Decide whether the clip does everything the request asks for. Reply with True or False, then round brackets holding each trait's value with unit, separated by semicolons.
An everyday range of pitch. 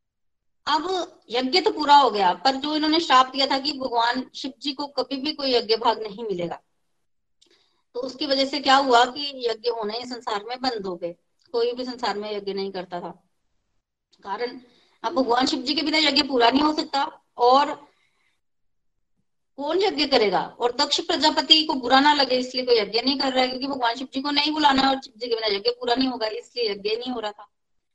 True (3.7 semitones)